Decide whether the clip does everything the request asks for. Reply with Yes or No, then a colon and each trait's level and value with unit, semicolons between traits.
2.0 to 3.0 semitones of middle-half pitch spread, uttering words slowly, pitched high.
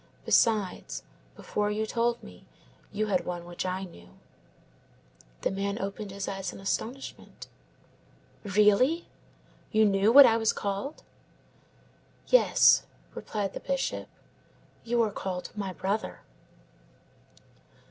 Yes: narrow, 2.6 semitones; slow, 115 wpm; high, 205 Hz